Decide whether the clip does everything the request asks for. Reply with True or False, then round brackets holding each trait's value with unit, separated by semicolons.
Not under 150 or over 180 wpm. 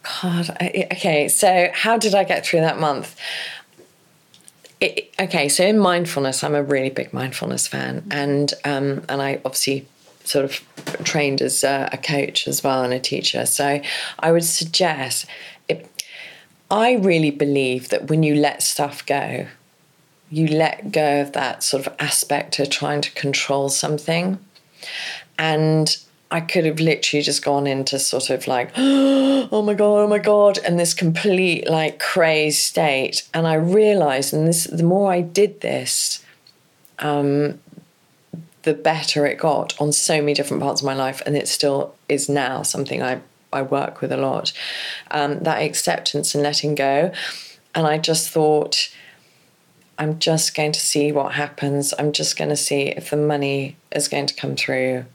True (170 wpm)